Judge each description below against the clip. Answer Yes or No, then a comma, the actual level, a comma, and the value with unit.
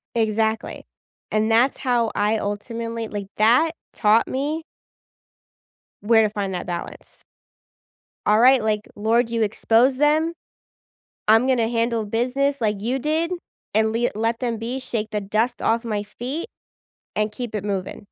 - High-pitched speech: Yes, high, 225 Hz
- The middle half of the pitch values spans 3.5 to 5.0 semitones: No, average, 2.7 semitones